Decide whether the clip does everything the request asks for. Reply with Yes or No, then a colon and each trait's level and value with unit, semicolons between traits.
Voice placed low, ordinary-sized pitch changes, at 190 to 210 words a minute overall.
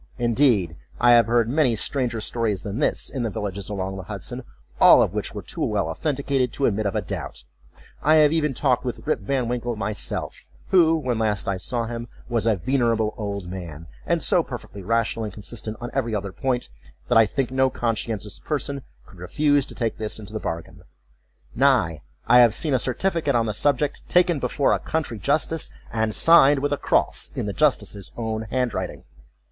Yes: low, 115 Hz; average, 4.5 semitones; average, 195 wpm